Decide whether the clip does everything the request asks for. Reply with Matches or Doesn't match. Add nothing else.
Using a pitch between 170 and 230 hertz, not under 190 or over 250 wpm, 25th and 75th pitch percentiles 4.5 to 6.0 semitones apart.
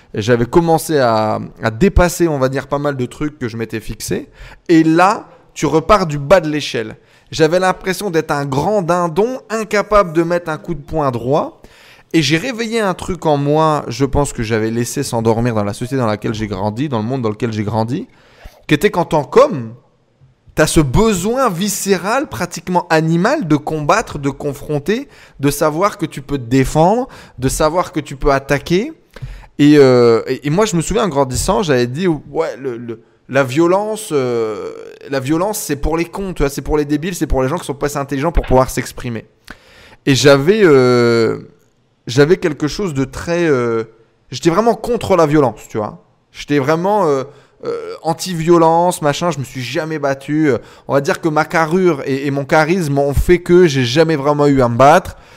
Doesn't match